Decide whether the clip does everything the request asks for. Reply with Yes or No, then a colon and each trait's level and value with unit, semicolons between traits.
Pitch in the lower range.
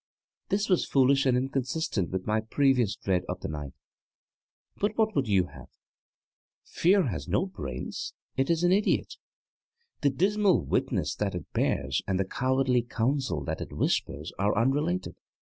Yes: low, 130 Hz